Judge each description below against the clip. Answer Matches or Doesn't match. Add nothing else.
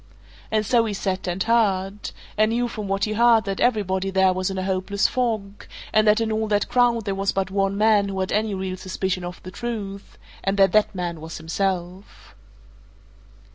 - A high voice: Matches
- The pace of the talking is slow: Doesn't match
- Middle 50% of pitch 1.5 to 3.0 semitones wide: Matches